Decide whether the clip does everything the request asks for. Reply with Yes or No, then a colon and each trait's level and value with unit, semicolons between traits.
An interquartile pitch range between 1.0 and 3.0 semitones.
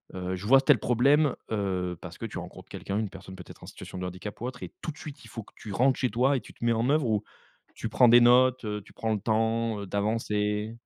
No: average, 3.4 semitones